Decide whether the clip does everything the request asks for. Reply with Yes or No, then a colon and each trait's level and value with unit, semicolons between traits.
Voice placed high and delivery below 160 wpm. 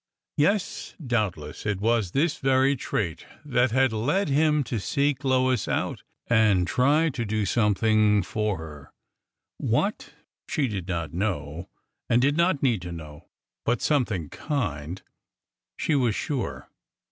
No: low, 115 Hz; average, 140 wpm